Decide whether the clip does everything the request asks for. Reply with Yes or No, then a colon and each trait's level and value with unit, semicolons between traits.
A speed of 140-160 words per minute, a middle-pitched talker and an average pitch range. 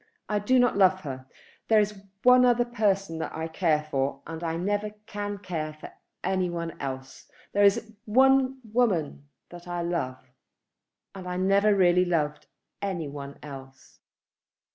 Yes: average, 155 wpm; medium, 180 Hz; average, 4.9 semitones